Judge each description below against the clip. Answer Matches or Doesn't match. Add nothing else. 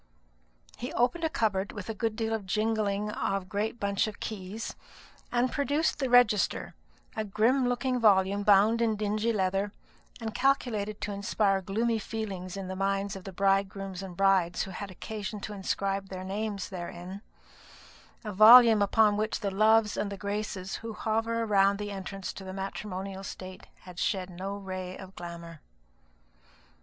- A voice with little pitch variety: Matches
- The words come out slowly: Doesn't match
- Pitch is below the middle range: Doesn't match